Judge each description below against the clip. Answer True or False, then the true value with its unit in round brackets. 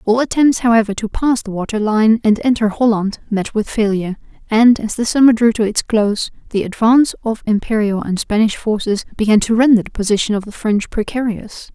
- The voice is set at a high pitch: True (220 Hz)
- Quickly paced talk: False (195 wpm)